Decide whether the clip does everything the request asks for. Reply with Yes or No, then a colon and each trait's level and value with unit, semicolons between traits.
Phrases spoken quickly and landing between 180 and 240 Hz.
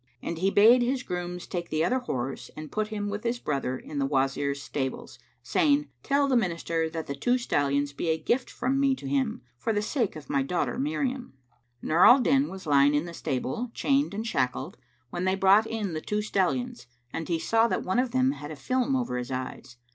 Yes: fast, 215 wpm; high, 190 Hz